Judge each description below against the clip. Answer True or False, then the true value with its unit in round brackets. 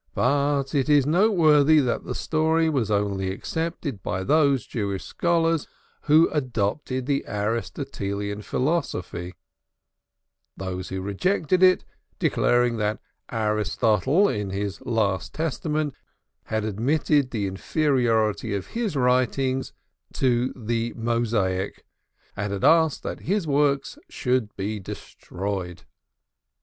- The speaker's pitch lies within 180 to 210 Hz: False (125 Hz)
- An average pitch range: False (6.5 semitones)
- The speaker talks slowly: True (110 wpm)